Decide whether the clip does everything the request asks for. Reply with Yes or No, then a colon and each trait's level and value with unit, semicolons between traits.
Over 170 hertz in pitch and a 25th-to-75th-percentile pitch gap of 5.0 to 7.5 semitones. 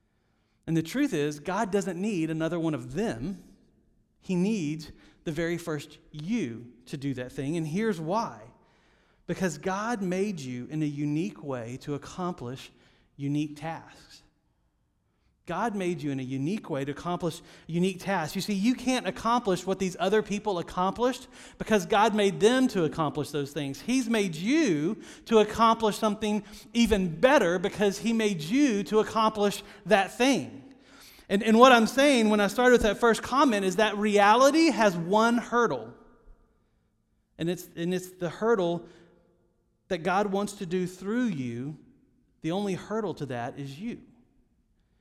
Yes: high, 190 Hz; wide, 5.5 semitones